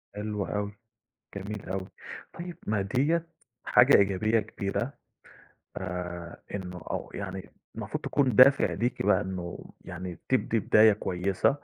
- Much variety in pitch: No, average, 3.5 semitones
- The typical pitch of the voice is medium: No, low, 100 Hz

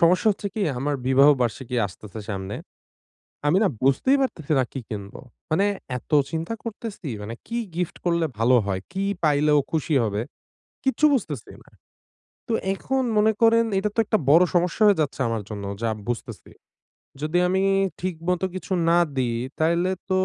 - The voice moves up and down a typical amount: No, wide, 7.3 semitones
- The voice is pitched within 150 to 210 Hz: Yes, medium, 160 Hz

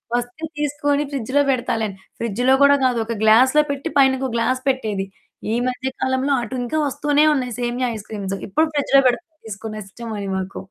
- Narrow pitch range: No, average, 4.1 semitones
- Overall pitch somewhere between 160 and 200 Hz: No, very high, 255 Hz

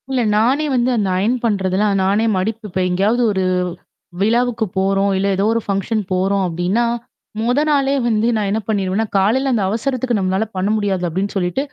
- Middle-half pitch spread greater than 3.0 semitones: Yes, average, 3.4 semitones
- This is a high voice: Yes, high, 205 Hz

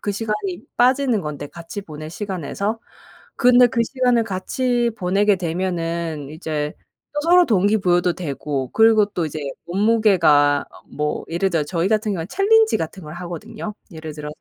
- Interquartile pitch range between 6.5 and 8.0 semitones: No, wide, 5.6 semitones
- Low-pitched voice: No, medium, 185 Hz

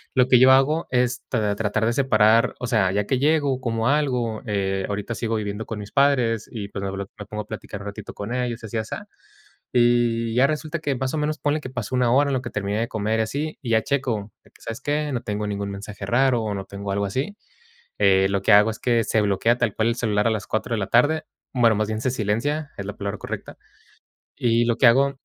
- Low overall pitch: Yes, low, 115 Hz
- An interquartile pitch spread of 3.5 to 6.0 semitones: Yes, average, 3.8 semitones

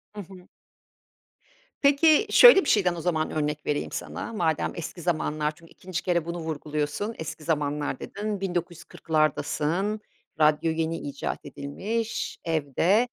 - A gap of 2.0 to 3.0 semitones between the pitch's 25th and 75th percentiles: No, average, 4.3 semitones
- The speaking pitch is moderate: Yes, medium, 165 Hz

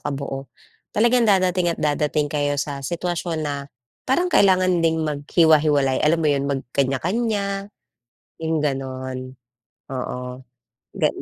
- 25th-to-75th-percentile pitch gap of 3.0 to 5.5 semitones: Yes, average, 4.5 semitones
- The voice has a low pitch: No, medium, 150 Hz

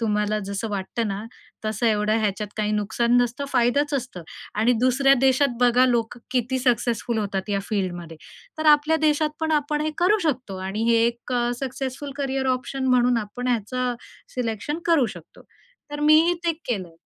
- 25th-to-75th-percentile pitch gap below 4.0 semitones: No, average, 4.3 semitones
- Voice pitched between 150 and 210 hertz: No, high, 245 Hz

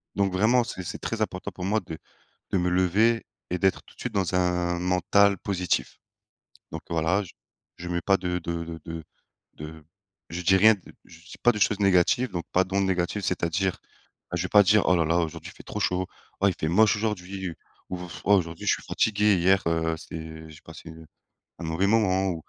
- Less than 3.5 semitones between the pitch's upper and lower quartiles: Yes, average, 2.9 semitones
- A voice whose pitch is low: Yes, very low, 90 Hz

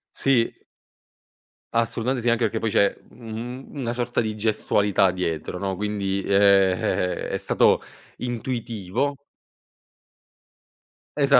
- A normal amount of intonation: Yes, average, 3.6 semitones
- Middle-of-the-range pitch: No, low, 110 Hz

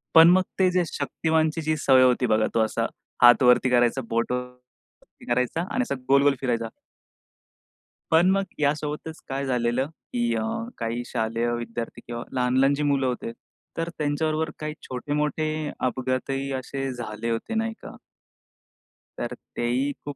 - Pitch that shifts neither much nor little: Yes, average, 4.0 semitones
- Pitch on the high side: No, low, 130 Hz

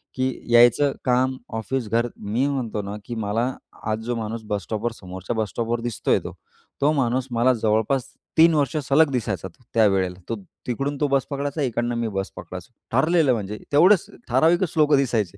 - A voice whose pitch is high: No, low, 120 Hz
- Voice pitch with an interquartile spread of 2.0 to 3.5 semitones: No, average, 4.1 semitones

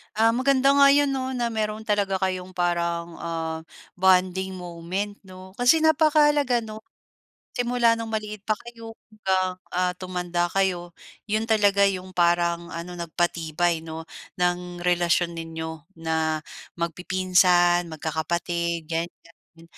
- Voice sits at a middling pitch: Yes, medium, 180 Hz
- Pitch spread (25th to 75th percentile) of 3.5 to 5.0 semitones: Yes, average, 4.1 semitones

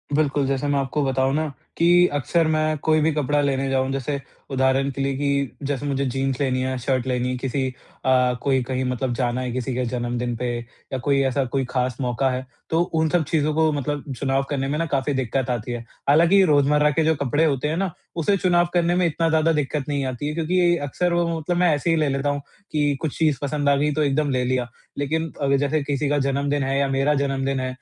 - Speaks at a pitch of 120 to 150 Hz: Yes, medium, 140 Hz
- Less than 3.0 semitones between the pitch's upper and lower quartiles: Yes, narrow, 2.6 semitones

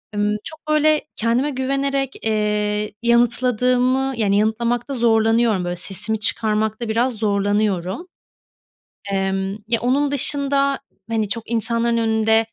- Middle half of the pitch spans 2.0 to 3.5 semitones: Yes, average, 3.2 semitones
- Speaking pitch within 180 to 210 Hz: No, high, 230 Hz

